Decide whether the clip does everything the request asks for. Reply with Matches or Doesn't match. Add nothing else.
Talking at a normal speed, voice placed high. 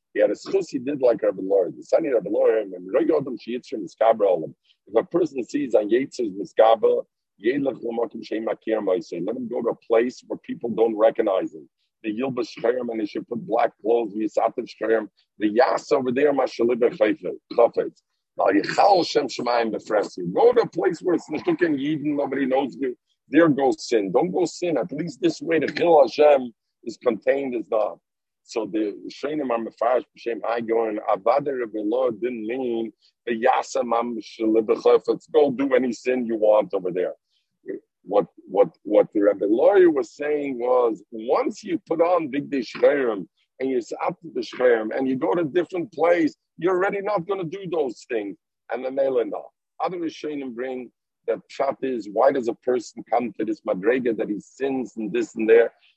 Matches